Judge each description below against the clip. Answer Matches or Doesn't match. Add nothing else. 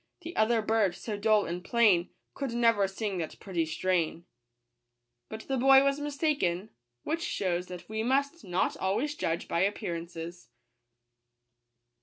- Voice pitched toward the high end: Matches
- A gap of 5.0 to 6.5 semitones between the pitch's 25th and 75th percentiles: Matches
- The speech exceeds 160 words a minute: Doesn't match